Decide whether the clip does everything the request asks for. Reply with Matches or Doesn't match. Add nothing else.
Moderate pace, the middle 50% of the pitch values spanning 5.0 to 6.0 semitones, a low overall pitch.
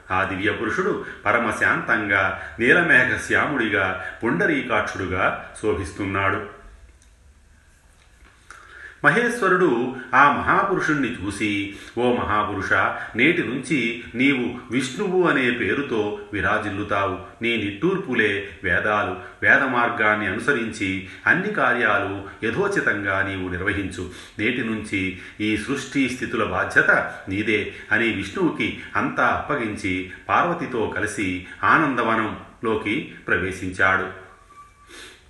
Doesn't match